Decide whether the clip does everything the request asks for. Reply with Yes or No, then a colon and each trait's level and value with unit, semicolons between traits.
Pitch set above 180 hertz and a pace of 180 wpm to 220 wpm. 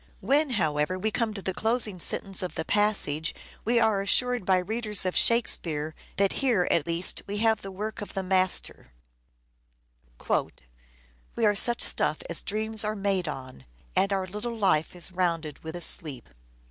No: high, 190 Hz; average, 170 wpm